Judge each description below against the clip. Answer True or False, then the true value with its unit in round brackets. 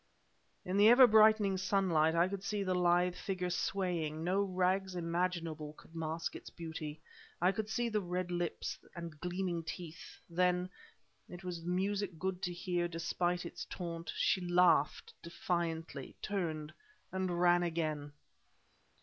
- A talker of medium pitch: True (175 Hz)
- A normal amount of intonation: False (2.0 semitones)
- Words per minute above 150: False (145 wpm)